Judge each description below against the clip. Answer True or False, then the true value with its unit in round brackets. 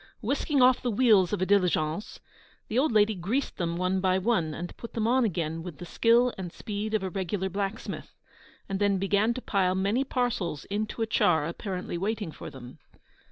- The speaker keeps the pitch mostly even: False (3.8 semitones)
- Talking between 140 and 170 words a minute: False (195 wpm)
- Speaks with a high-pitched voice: True (200 Hz)